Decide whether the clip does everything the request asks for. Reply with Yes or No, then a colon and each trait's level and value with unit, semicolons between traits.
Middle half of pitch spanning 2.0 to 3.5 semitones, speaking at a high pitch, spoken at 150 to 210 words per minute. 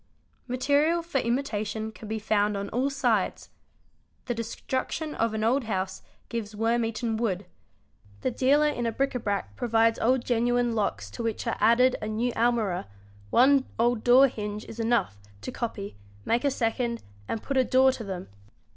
Yes: average, 2.9 semitones; high, 230 Hz; average, 170 wpm